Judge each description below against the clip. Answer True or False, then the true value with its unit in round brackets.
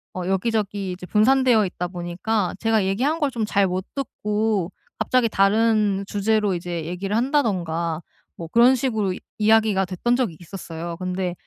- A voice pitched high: True (200 Hz)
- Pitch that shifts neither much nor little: True (3.7 semitones)